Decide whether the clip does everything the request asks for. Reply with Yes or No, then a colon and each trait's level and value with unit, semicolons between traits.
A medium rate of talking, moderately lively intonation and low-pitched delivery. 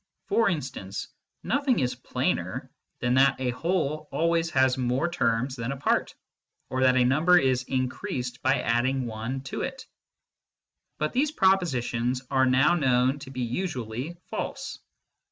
Yes: average, 150 wpm; average, 4.1 semitones; low, 130 Hz